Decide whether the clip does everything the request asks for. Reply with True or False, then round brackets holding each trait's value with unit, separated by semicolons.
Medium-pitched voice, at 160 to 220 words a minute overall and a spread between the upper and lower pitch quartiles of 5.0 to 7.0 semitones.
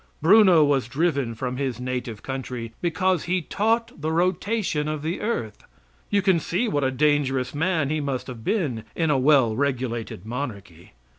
True (145 Hz; 165 wpm; 5.4 semitones)